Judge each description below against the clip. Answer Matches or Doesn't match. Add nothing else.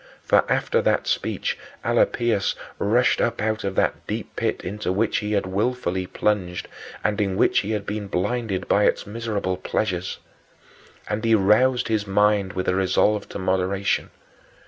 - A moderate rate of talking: Matches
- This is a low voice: Matches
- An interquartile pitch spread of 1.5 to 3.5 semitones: Matches